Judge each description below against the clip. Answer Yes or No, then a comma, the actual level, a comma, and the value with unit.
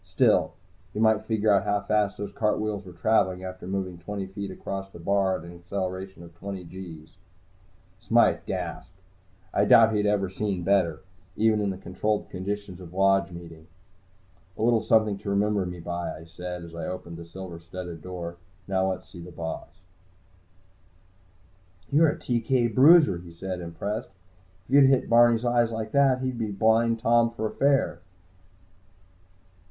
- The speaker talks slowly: No, average, 165 wpm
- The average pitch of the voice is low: Yes, very low, 95 Hz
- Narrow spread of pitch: No, average, 3.6 semitones